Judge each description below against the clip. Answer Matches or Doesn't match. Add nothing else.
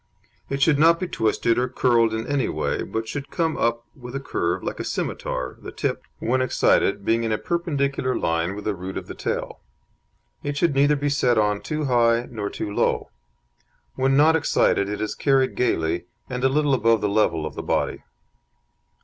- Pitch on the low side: Matches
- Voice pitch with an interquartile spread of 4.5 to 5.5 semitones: Matches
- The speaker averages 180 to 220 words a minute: Matches